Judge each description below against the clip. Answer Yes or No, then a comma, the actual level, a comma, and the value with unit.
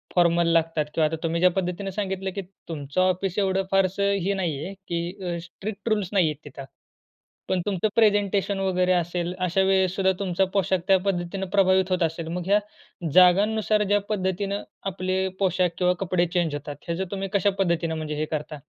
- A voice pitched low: No, medium, 185 Hz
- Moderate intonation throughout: No, narrow, 2.3 semitones